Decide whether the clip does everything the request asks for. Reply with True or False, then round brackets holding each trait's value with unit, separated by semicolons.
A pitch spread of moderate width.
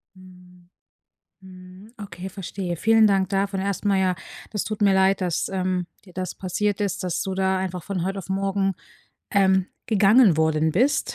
False (1.4 semitones)